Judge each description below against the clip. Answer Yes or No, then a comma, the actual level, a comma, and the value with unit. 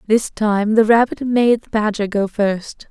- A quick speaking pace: No, average, 185 wpm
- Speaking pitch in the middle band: No, high, 215 Hz